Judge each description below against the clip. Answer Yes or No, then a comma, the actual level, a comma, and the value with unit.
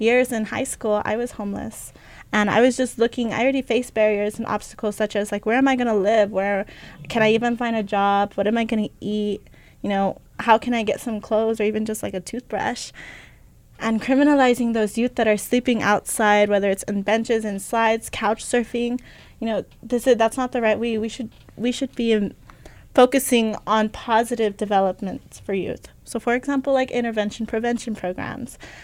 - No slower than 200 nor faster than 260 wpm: Yes, fast, 205 wpm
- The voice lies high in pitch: Yes, high, 225 Hz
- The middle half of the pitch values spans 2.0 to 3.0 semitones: Yes, narrow, 2.4 semitones